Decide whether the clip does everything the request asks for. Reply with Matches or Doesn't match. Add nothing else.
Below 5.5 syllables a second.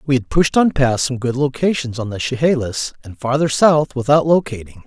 Matches